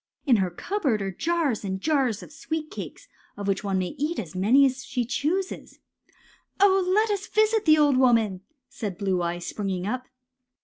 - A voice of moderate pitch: No, very high, 255 Hz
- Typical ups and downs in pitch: No, wide, 8.4 semitones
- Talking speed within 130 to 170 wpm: No, average, 185 wpm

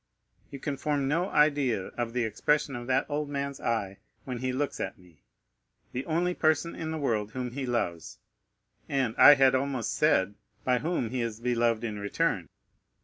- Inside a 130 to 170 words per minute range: No, average, 180 wpm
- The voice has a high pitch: No, low, 130 Hz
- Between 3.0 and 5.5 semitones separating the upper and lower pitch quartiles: Yes, average, 4.0 semitones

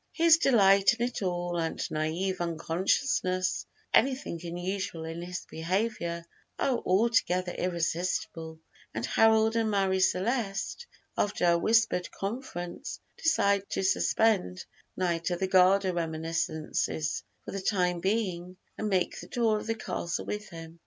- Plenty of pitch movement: No, average, 4.0 semitones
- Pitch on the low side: No, medium, 185 Hz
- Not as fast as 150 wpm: Yes, slow, 135 wpm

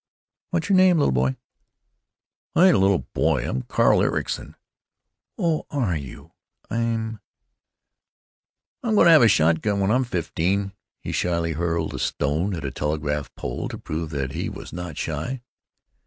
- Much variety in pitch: Yes, wide, 7.3 semitones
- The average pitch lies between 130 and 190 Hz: No, very low, 90 Hz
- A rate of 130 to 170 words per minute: Yes, average, 150 wpm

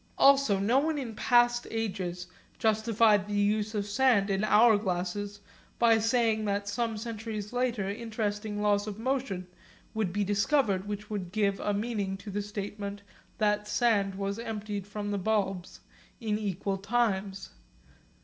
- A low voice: No, high, 210 Hz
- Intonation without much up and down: Yes, narrow, 2.0 semitones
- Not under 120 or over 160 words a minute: Yes, average, 150 wpm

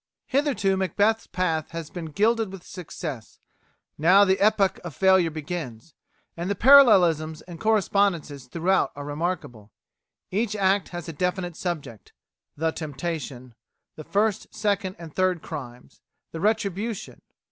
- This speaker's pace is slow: Yes, slow, 130 wpm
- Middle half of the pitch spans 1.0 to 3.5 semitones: No, average, 4.2 semitones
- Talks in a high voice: No, medium, 180 Hz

